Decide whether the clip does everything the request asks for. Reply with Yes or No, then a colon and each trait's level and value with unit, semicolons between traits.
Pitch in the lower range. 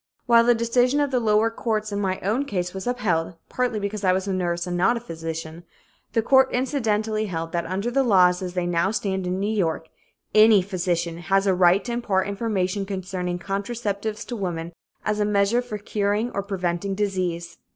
No: high, 200 Hz